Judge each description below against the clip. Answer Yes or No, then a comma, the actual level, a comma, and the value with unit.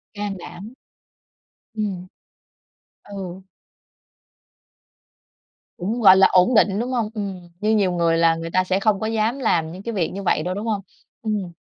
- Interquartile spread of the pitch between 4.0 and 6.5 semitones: No, average, 3.0 semitones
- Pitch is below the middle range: No, high, 195 Hz